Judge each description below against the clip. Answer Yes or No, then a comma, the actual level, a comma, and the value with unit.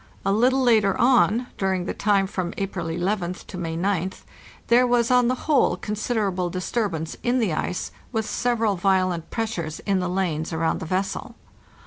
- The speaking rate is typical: Yes, average, 165 wpm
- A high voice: Yes, high, 195 Hz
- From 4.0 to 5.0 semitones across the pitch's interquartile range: Yes, average, 4.4 semitones